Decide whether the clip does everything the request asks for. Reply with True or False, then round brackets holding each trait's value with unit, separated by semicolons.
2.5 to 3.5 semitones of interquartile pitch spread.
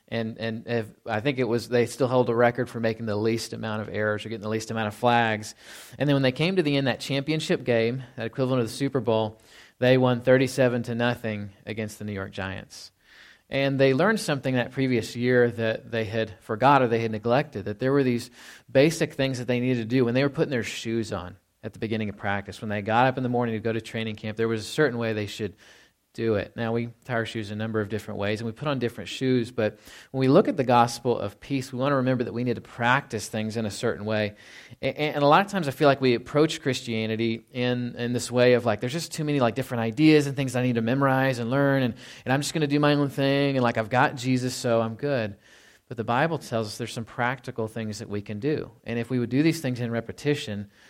True (3.1 semitones)